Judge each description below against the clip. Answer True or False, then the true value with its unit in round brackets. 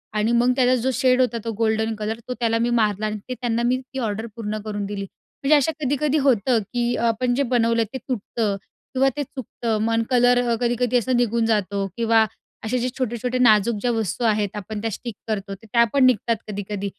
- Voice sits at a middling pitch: False (230 Hz)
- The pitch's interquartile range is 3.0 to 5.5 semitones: False (2.6 semitones)